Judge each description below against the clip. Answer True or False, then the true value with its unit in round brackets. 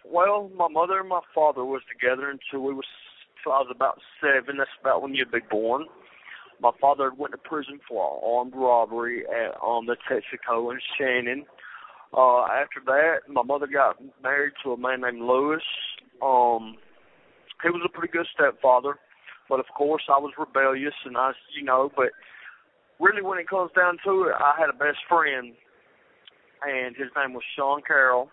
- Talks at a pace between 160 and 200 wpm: True (170 wpm)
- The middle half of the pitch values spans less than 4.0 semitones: True (2.8 semitones)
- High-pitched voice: False (135 Hz)